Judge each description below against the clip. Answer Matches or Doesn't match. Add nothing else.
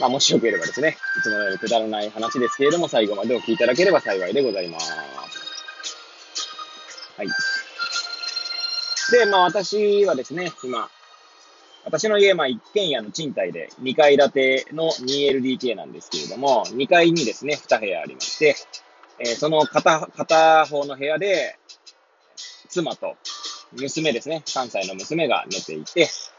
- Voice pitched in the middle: Matches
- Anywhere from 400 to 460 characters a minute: Doesn't match